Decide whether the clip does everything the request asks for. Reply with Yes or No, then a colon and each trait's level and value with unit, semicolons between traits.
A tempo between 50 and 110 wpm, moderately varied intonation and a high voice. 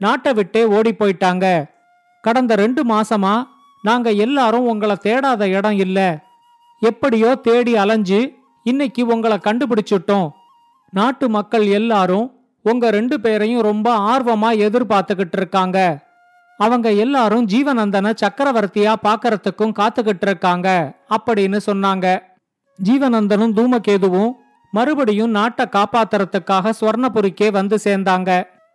Yes: average, 95 wpm; average, 3.0 semitones; high, 220 Hz